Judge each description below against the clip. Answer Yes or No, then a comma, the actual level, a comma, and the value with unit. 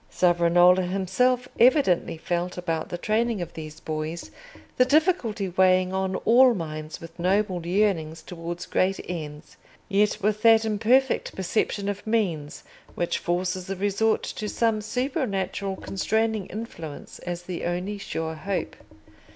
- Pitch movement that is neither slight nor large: Yes, average, 3.8 semitones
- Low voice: No, high, 190 Hz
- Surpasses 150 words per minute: No, slow, 135 wpm